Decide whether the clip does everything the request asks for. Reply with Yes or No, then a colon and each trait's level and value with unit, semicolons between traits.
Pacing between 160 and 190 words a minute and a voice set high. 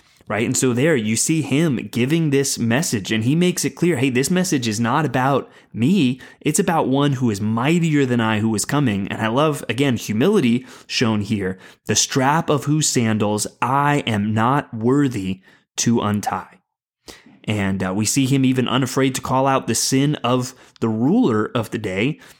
No: average, 185 wpm; low, 125 Hz